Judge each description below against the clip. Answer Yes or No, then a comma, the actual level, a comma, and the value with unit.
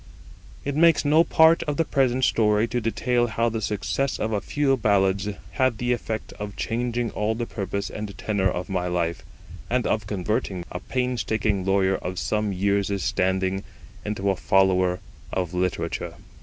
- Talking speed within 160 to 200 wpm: Yes, average, 165 wpm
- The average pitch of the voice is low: Yes, low, 105 Hz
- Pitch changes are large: No, average, 4.0 semitones